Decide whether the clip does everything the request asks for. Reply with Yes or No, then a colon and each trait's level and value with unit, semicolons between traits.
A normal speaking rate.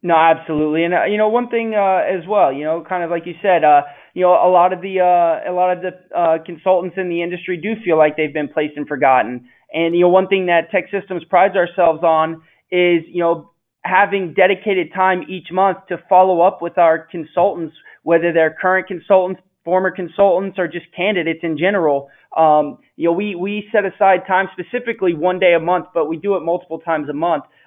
No: fast, 215 wpm